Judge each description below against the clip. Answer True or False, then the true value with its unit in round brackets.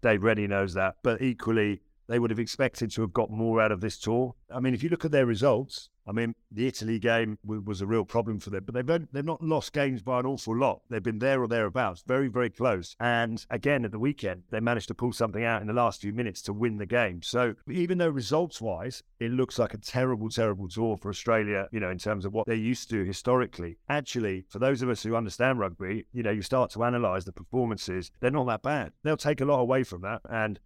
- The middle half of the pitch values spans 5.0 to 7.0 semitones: False (3.2 semitones)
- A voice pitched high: False (115 Hz)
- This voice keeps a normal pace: False (250 wpm)